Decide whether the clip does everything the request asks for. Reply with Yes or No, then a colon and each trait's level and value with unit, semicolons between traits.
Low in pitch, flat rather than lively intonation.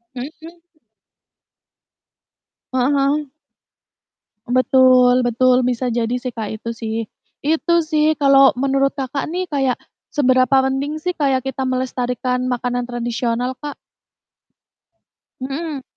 No: very high, 260 Hz; narrow, 2.1 semitones